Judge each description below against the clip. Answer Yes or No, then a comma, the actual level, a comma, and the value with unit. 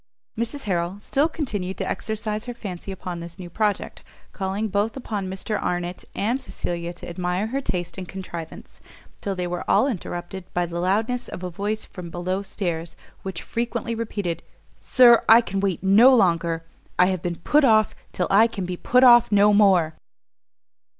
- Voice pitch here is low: No, high, 195 Hz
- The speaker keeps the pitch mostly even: No, average, 3.9 semitones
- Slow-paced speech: No, average, 175 wpm